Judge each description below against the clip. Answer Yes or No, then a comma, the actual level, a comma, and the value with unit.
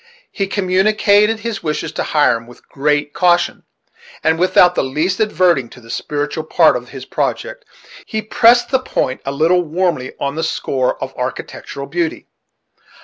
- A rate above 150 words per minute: Yes, average, 160 wpm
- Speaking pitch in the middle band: Yes, medium, 165 Hz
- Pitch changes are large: Yes, wide, 5.9 semitones